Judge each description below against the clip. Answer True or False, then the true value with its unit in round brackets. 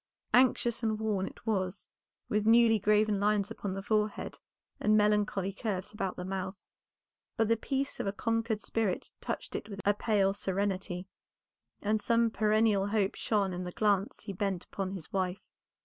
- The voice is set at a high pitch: True (205 Hz)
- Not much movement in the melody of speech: True (2.0 semitones)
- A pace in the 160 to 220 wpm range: True (165 wpm)